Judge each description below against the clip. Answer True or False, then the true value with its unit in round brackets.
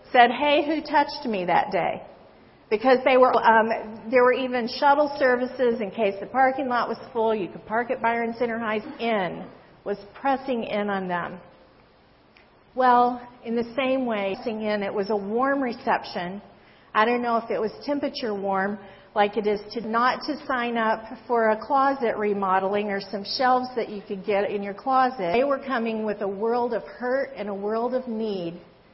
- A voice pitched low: False (230 Hz)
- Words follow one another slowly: False (190 wpm)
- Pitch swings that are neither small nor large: True (3.6 semitones)